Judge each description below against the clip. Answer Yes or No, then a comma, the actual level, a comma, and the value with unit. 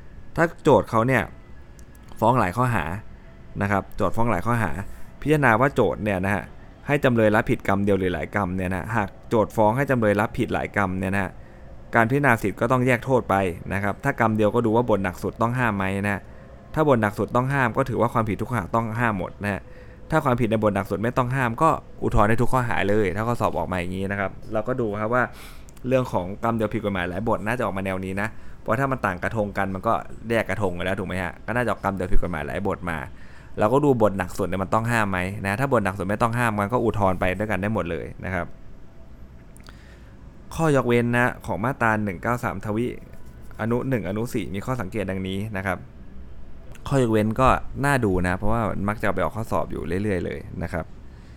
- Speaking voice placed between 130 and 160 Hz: No, low, 105 Hz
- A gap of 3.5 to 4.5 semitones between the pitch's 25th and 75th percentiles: Yes, average, 4.0 semitones